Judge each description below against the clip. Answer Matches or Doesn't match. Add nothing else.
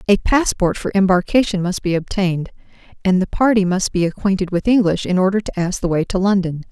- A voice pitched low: Doesn't match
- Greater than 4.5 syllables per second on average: Matches